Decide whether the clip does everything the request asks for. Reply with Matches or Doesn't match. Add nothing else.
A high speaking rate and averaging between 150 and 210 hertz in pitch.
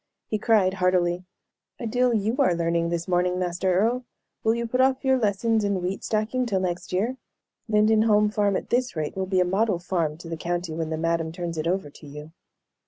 Matches